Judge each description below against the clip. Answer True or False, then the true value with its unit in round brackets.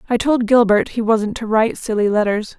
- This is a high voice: True (225 Hz)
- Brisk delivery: True (210 wpm)